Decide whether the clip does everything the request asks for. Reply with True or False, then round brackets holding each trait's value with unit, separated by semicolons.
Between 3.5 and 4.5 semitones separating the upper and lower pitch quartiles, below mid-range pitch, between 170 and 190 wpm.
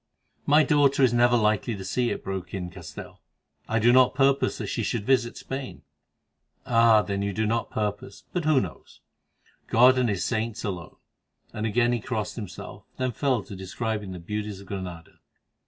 True (3.9 semitones; 110 Hz; 175 wpm)